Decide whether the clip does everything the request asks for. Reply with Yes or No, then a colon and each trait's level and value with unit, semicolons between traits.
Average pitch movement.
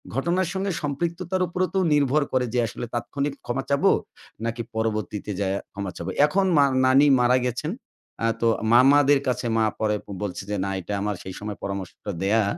No: wide, 5.7 semitones